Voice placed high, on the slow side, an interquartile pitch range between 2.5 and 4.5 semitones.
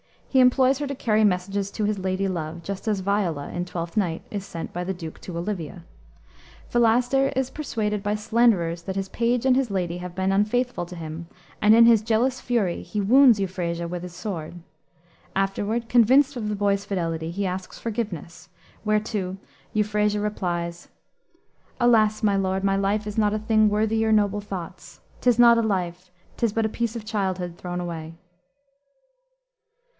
No: high, 205 Hz; average, 175 wpm; average, 3.8 semitones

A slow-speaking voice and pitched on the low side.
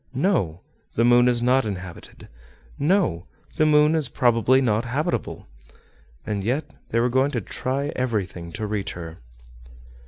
No: average, 145 wpm; low, 120 Hz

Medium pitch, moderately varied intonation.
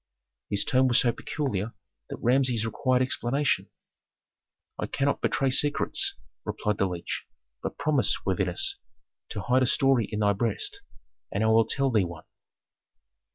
No: low, 125 Hz; average, 4.2 semitones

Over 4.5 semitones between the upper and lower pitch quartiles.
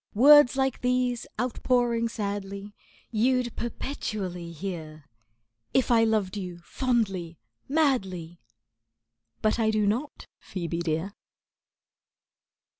Yes: average, 5.2 semitones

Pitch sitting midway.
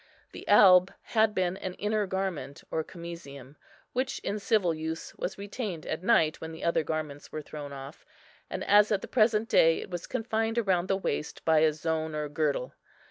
Yes: medium, 175 Hz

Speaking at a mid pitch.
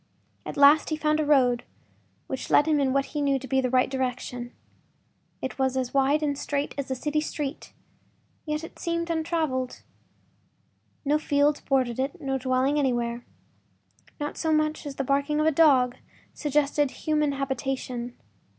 No: very high, 280 Hz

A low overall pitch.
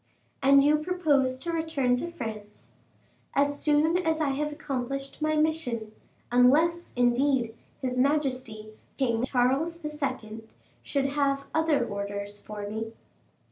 No: very high, 275 Hz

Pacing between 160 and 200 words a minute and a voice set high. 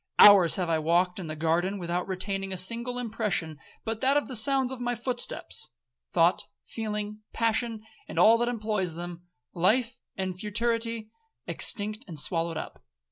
No: average, 150 wpm; high, 205 Hz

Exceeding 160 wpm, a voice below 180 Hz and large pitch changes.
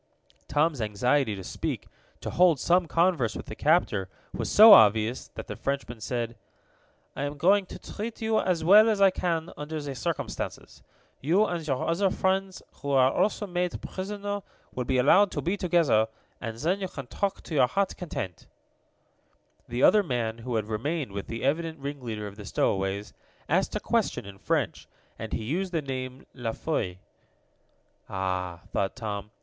Yes: average, 175 wpm; medium, 140 Hz; wide, 8.2 semitones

